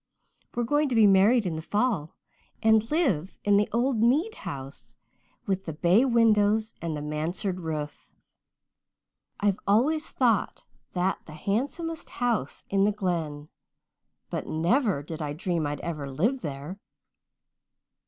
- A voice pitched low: No, high, 200 Hz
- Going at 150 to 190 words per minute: No, average, 140 wpm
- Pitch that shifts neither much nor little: No, wide, 6.7 semitones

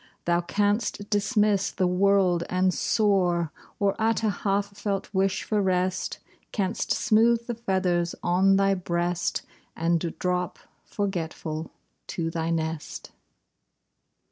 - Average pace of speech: No, slow, 115 wpm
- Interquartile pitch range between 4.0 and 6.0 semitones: No, average, 2.8 semitones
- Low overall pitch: No, high, 190 Hz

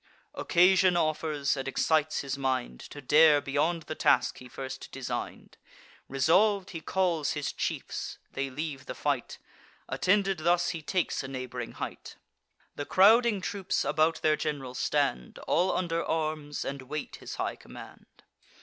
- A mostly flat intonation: No, average, 4.2 semitones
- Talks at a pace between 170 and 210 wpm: No, average, 145 wpm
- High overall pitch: No, medium, 155 Hz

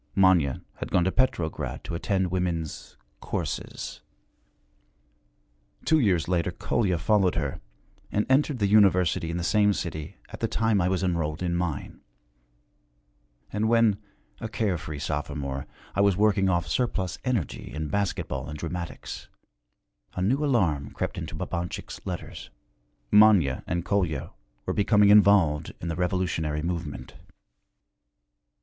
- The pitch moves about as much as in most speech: Yes, average, 4.1 semitones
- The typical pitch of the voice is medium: No, very low, 90 Hz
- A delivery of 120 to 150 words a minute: Yes, slow, 135 wpm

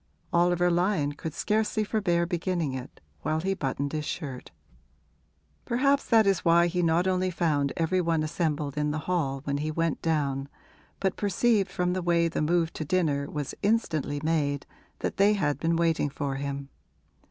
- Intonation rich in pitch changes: No, average, 3.8 semitones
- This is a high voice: No, medium, 165 Hz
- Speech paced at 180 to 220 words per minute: No, average, 170 wpm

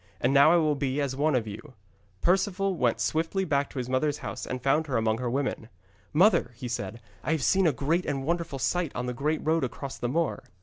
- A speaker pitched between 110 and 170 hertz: Yes, medium, 140 Hz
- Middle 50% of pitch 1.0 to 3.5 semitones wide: No, average, 4.3 semitones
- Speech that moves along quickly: Yes, fast, 230 wpm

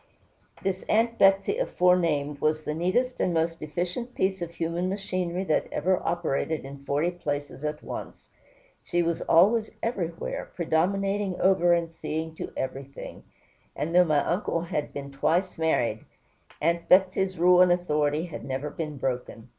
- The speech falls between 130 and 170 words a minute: Yes, average, 150 wpm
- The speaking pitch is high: No, medium, 170 Hz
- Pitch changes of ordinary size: Yes, average, 3.5 semitones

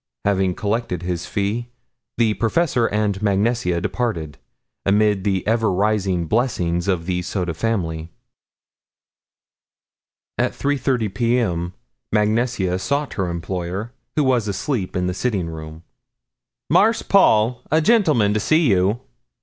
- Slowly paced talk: Yes, slow, 125 wpm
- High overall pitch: No, low, 105 Hz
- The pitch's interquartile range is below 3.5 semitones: No, average, 4.7 semitones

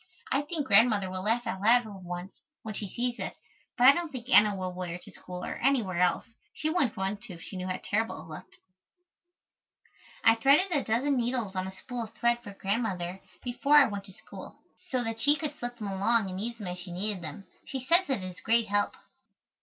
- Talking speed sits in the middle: No, fast, 230 wpm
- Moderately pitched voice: No, high, 220 Hz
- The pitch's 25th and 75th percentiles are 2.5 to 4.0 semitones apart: No, average, 4.6 semitones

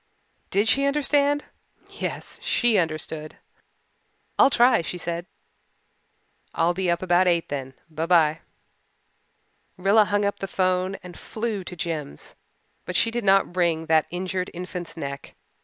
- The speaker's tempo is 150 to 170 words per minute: No, average, 140 wpm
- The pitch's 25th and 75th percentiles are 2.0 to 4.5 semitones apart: Yes, average, 3.5 semitones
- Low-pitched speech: No, medium, 180 Hz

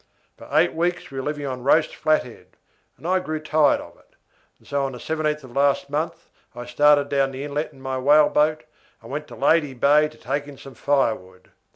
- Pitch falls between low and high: Yes, medium, 145 Hz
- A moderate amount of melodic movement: No, narrow, 2.3 semitones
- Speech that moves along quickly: Yes, fast, 210 wpm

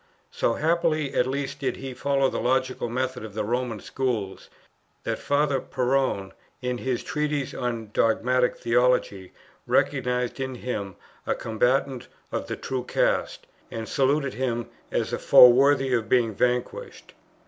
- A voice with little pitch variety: Yes, narrow, 2.2 semitones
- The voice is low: Yes, low, 125 Hz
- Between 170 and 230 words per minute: No, average, 145 wpm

